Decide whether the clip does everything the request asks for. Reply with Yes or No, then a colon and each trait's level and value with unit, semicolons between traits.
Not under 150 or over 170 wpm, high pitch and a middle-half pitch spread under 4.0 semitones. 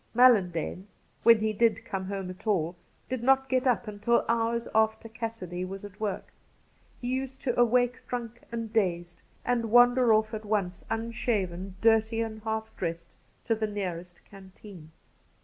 Yes: average, 160 wpm; high, 220 Hz; average, 3.5 semitones